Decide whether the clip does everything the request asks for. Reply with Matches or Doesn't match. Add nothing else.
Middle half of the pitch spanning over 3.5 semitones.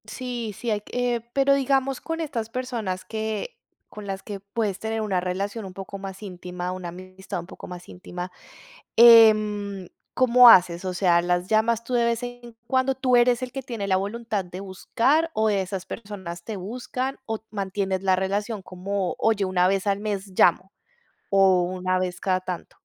Matches